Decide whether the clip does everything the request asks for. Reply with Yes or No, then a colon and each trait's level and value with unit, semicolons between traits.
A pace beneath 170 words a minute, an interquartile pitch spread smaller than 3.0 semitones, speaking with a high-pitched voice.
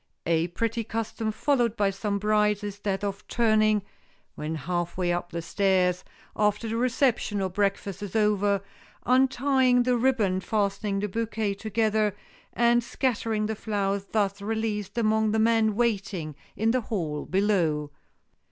Yes: average, 145 wpm; narrow, 2.5 semitones; high, 210 Hz